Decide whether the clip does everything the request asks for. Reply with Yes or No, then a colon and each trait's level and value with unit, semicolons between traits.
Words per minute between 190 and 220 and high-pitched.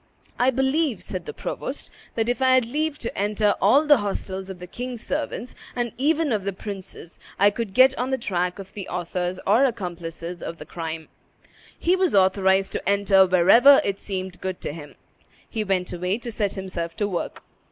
Yes: average, 195 wpm; high, 200 Hz